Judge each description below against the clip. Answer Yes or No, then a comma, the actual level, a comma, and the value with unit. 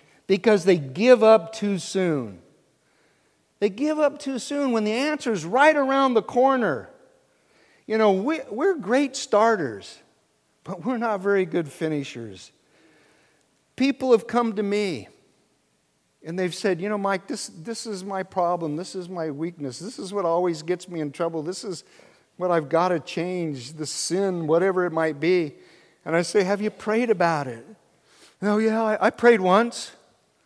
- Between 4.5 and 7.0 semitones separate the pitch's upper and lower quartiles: Yes, average, 5.3 semitones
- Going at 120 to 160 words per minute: No, average, 170 wpm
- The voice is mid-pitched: No, high, 195 Hz